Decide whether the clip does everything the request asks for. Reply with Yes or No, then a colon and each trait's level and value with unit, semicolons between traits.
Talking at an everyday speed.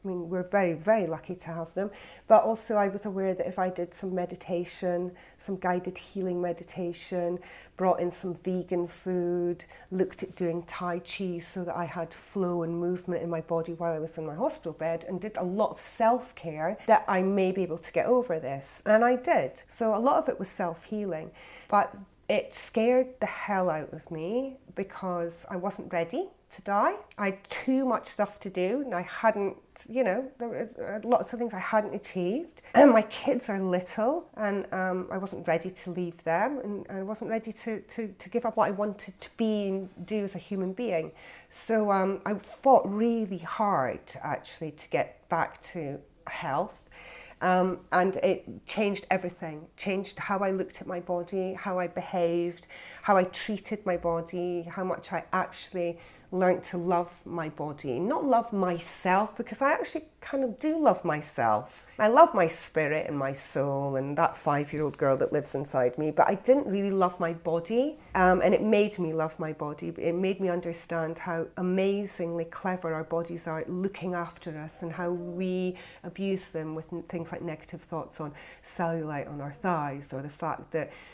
Yes: average, 195 wpm